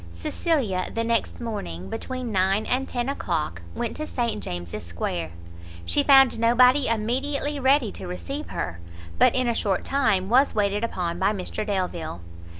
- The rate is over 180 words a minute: No, average, 155 wpm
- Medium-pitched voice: No, high, 225 Hz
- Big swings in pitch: Yes, wide, 5.9 semitones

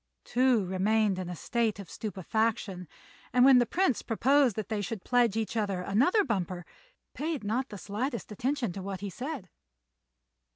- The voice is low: No, high, 220 Hz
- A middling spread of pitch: Yes, average, 4.2 semitones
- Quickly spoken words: No, average, 170 wpm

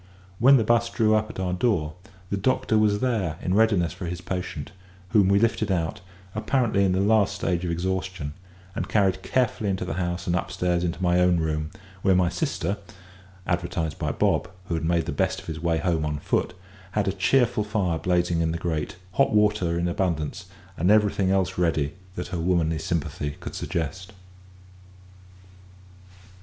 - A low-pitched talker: Yes, very low, 90 Hz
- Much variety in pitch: No, average, 3.5 semitones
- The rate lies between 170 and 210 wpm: Yes, average, 180 wpm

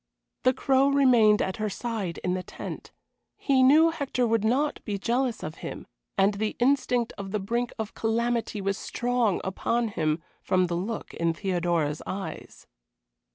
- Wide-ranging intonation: No, average, 4.4 semitones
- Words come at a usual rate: Yes, average, 160 wpm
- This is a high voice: Yes, high, 220 Hz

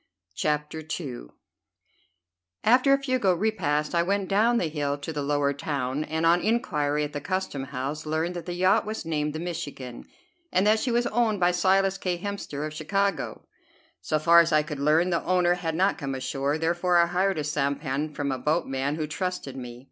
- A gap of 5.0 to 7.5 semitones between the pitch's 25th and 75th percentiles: No, average, 4.3 semitones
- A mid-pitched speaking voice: Yes, medium, 160 Hz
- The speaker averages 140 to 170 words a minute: No, average, 195 wpm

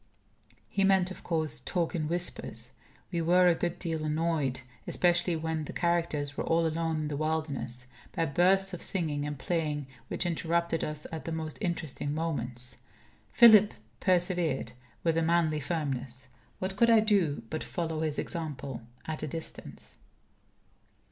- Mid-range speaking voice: Yes, medium, 160 Hz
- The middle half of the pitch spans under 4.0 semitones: Yes, narrow, 2.6 semitones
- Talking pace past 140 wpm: Yes, average, 155 wpm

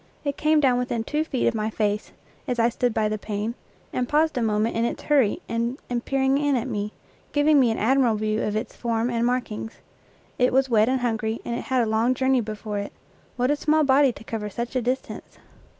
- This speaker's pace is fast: Yes, fast, 225 wpm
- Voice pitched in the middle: No, high, 240 Hz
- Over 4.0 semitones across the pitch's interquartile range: No, average, 3.3 semitones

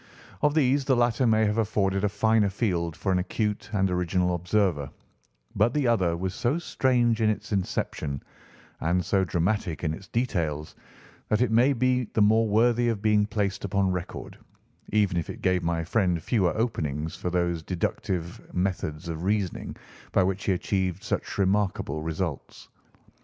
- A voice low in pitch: Yes, very low, 95 Hz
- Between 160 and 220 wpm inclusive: Yes, average, 165 wpm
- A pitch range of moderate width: Yes, average, 4.1 semitones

